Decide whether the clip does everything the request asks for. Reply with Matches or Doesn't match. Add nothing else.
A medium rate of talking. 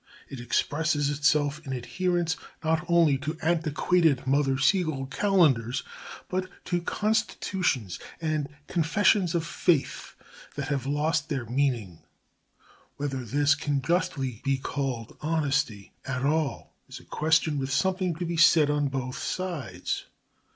Doesn't match